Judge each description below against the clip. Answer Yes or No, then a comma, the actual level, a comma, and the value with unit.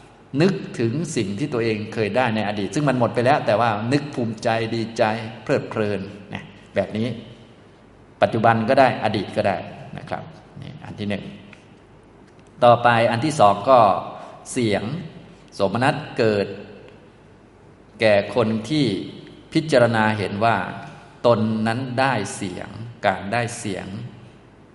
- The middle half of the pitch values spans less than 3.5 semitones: Yes, average, 3.1 semitones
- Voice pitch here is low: Yes, low, 115 Hz